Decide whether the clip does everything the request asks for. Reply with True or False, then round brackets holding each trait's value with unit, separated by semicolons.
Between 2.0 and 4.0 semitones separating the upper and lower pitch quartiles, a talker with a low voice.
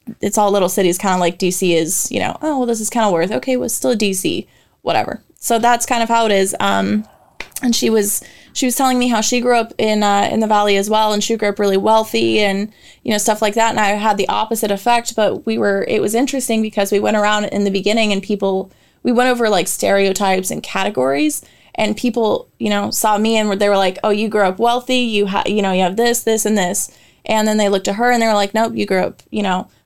False (2.6 semitones; 210 Hz)